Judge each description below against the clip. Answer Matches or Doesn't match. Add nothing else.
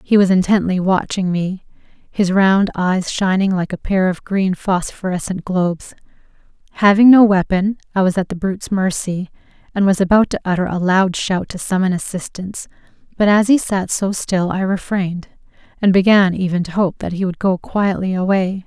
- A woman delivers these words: Matches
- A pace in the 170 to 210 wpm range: Matches